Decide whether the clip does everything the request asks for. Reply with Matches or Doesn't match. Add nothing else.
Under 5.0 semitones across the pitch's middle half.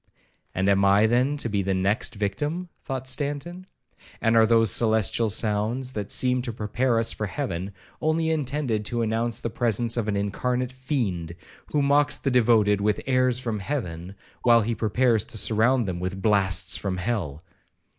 Matches